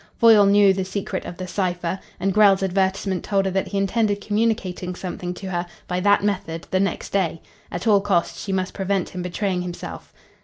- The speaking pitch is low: No, high, 190 Hz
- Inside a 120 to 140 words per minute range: No, average, 195 wpm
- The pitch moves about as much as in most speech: No, narrow, 1.9 semitones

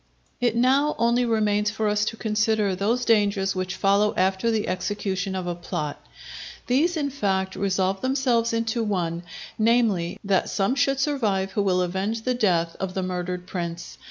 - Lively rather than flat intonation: No, average, 3.6 semitones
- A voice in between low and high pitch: No, high, 205 Hz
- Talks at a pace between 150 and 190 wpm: Yes, average, 165 wpm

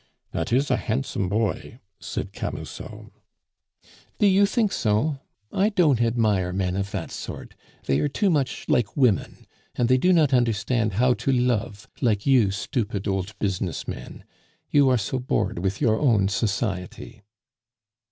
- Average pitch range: Yes, average, 5.0 semitones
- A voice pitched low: Yes, low, 115 Hz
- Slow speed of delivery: No, average, 150 wpm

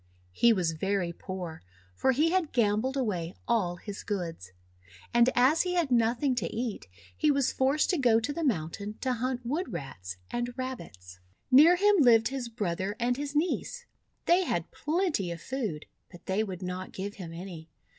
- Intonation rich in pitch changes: Yes, wide, 6.8 semitones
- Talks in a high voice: Yes, high, 230 Hz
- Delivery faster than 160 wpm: Yes, average, 175 wpm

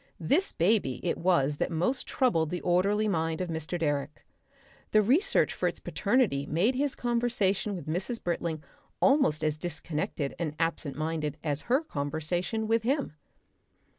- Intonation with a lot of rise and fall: Yes, wide, 6.3 semitones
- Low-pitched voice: No, medium, 175 Hz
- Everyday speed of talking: Yes, average, 150 wpm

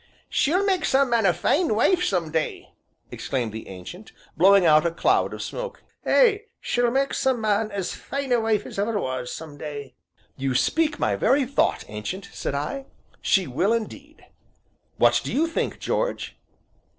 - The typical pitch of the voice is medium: No, high, 215 Hz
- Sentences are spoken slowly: No, average, 170 wpm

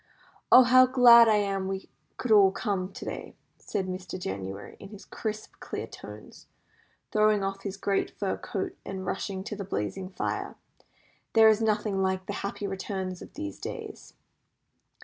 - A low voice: No, high, 195 Hz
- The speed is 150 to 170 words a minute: Yes, average, 165 wpm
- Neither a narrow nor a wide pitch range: No, narrow, 2.1 semitones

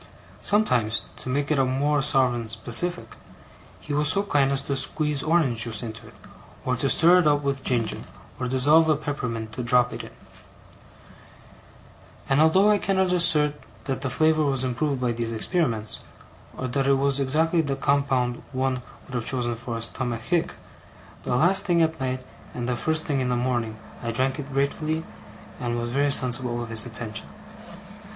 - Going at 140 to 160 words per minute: No, average, 175 wpm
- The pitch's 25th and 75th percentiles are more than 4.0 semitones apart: No, average, 3.7 semitones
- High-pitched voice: No, low, 135 Hz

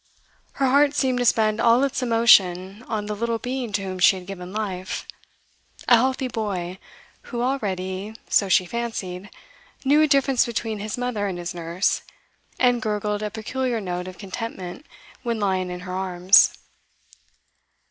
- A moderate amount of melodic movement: Yes, average, 4.5 semitones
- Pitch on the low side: No, high, 210 Hz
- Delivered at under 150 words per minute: No, average, 155 wpm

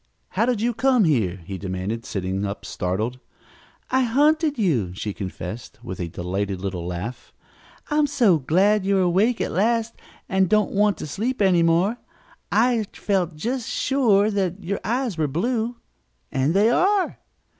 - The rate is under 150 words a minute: No, average, 155 wpm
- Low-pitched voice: No, high, 190 Hz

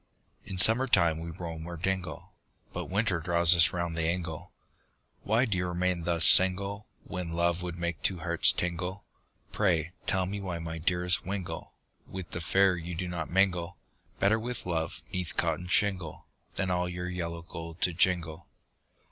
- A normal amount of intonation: No, narrow, 2.0 semitones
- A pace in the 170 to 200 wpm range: Yes, average, 175 wpm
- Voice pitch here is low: Yes, very low, 90 Hz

